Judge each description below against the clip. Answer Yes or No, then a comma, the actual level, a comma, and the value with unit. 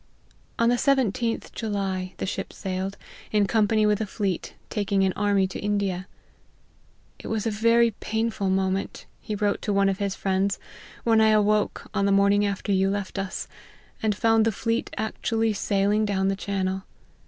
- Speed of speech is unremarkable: Yes, average, 180 wpm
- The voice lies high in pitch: Yes, high, 205 Hz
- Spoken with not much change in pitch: Yes, narrow, 2.1 semitones